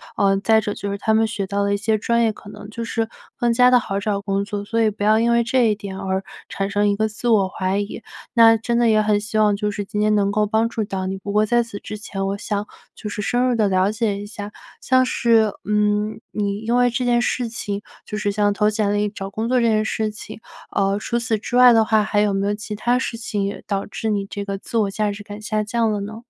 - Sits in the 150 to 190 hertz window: No, high, 210 Hz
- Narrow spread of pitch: Yes, narrow, 2.0 semitones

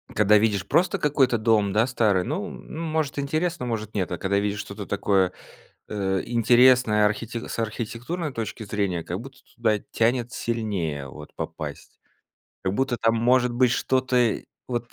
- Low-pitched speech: Yes, low, 115 Hz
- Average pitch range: Yes, average, 3.8 semitones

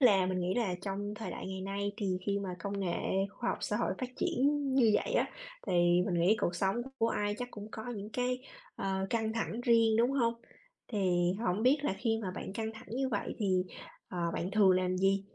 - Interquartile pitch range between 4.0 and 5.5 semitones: No, average, 3.1 semitones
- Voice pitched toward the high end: Yes, high, 205 Hz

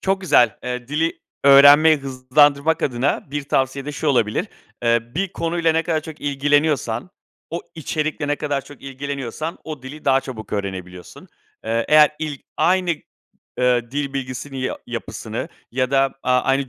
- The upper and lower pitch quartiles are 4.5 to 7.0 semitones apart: No, average, 3.2 semitones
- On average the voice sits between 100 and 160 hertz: Yes, medium, 140 Hz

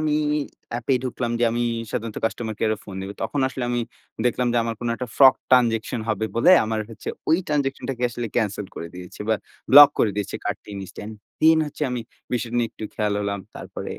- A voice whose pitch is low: Yes, low, 120 Hz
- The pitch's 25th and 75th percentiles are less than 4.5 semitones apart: Yes, average, 2.8 semitones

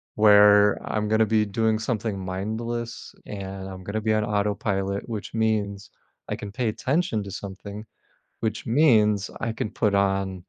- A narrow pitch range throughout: Yes, narrow, 1.9 semitones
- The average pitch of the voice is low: Yes, low, 105 Hz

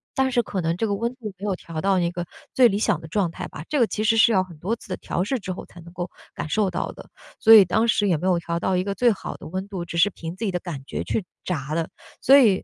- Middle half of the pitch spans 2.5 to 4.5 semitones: Yes, average, 4.1 semitones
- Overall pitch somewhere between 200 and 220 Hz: No, high, 190 Hz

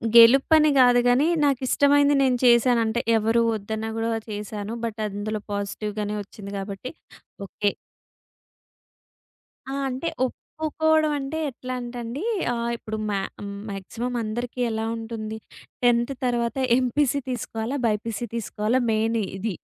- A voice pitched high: Yes, high, 235 Hz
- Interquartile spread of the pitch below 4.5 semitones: Yes, average, 2.8 semitones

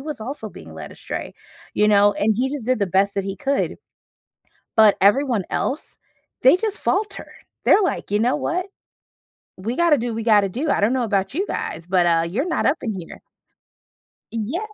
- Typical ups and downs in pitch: No, wide, 6.3 semitones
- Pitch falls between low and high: No, high, 230 Hz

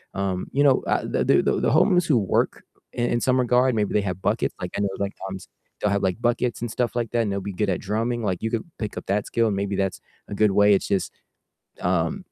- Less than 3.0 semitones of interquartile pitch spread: No, average, 3.3 semitones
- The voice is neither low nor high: No, low, 105 Hz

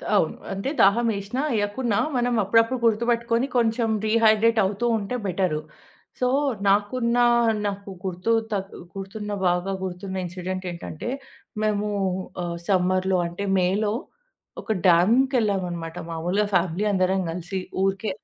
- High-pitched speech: Yes, high, 200 Hz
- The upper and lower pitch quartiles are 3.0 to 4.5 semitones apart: Yes, average, 3.5 semitones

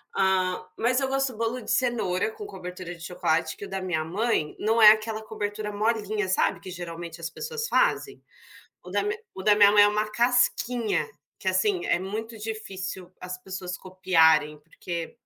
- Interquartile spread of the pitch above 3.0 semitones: Yes, average, 3.6 semitones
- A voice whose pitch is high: Yes, high, 205 Hz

